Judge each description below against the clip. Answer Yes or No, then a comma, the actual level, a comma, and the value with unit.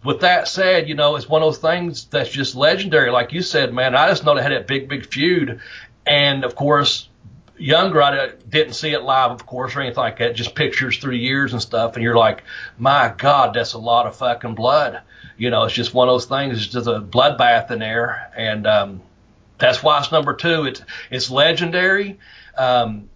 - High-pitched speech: No, low, 130 Hz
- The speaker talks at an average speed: No, fast, 215 wpm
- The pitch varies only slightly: No, average, 4.0 semitones